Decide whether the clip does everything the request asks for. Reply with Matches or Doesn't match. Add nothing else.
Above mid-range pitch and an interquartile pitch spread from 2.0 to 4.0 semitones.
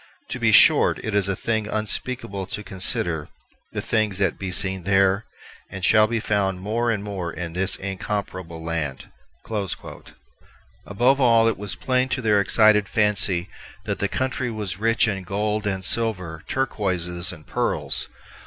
Doesn't match